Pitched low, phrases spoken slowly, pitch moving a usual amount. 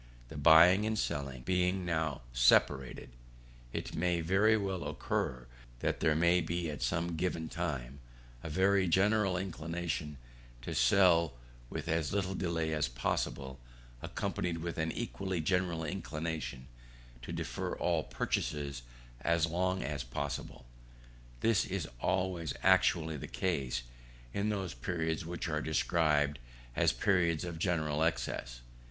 Yes: very low, 85 Hz; slow, 130 wpm; average, 3.7 semitones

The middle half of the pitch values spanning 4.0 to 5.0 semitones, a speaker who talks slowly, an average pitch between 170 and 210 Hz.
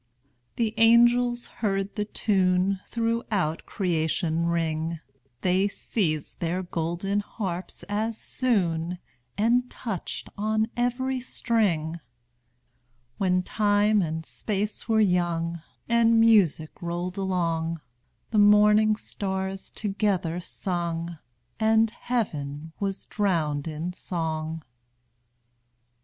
Yes: average, 4.4 semitones; slow, 95 wpm; high, 190 Hz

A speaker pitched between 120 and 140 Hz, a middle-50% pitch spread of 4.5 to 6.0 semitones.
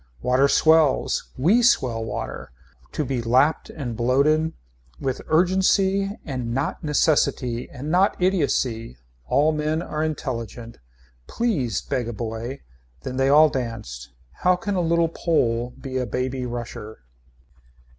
Yes: low, 135 Hz; average, 5.1 semitones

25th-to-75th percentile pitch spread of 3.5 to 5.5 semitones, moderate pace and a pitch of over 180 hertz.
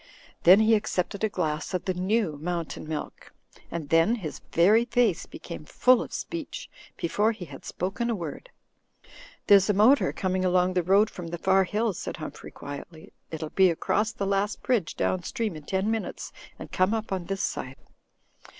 Yes: average, 4.1 semitones; average, 180 wpm; high, 190 Hz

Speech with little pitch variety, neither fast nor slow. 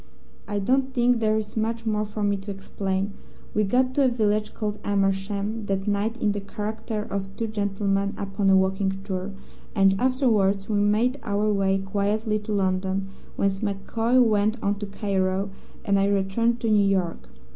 Yes: narrow, 1.9 semitones; average, 175 wpm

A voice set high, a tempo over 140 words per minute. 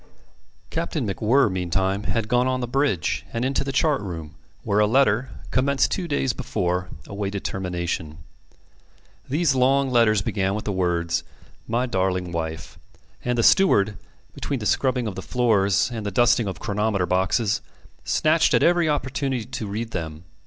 No: low, 110 Hz; average, 160 wpm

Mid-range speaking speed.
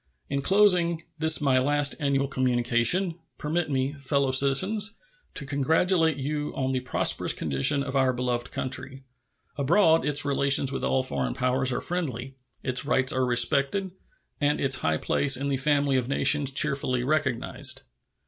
Yes: average, 150 wpm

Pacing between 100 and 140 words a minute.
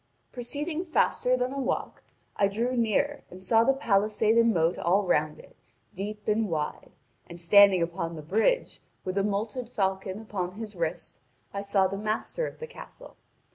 No: average, 175 wpm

